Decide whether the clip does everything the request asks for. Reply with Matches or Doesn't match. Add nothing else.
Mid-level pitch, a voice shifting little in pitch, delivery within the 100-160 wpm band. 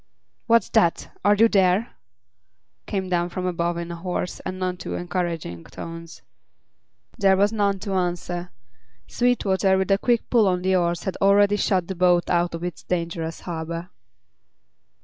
Matches